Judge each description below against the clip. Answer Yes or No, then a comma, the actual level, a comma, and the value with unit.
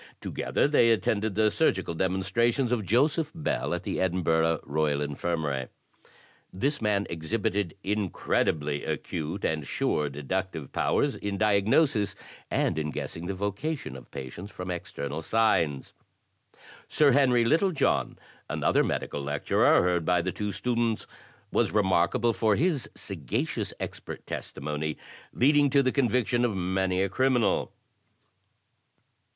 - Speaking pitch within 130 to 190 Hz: No, low, 100 Hz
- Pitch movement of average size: No, wide, 6.4 semitones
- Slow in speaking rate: Yes, slow, 125 wpm